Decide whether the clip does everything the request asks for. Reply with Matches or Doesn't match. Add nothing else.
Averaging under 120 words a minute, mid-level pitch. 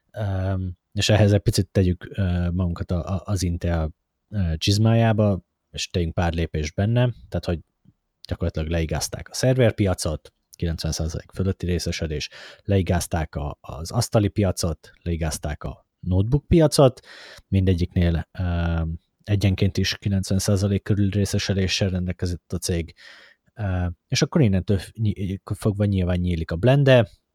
Doesn't match